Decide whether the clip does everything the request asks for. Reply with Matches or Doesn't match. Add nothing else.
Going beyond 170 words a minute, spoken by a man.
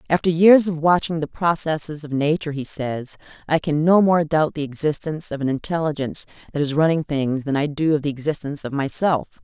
Doesn't match